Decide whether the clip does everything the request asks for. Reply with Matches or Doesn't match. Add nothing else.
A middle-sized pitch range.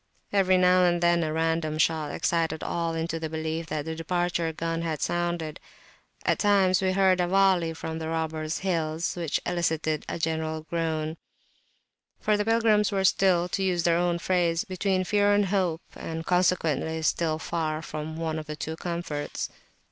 Doesn't match